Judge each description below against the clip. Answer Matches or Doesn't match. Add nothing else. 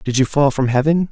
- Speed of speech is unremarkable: Doesn't match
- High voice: Doesn't match